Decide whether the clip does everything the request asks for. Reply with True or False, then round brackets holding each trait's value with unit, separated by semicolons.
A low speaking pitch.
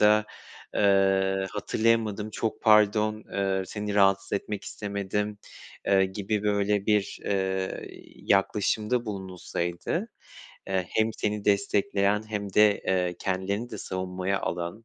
True (100 Hz)